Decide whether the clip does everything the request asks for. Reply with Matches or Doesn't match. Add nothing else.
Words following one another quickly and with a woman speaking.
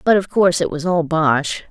Matches